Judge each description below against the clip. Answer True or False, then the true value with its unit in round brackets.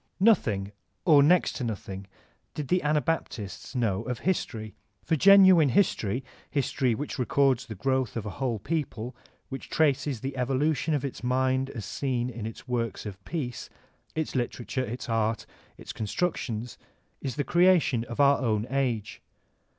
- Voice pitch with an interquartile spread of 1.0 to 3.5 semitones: False (4.5 semitones)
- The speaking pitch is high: False (130 Hz)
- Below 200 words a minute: True (160 wpm)